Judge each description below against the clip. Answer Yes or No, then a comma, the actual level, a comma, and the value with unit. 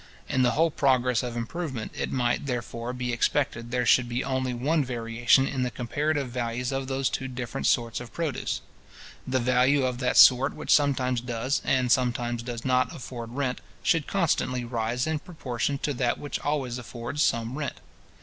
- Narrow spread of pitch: Yes, narrow, 2.2 semitones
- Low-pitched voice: Yes, low, 125 Hz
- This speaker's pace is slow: No, average, 180 wpm